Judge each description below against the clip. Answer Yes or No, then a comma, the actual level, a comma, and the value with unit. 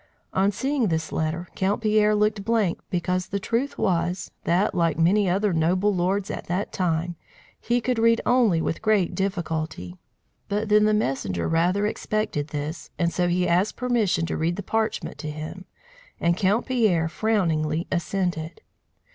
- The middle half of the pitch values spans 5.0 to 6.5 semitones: No, average, 4.1 semitones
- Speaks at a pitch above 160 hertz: Yes, medium, 185 Hz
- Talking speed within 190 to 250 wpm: No, average, 160 wpm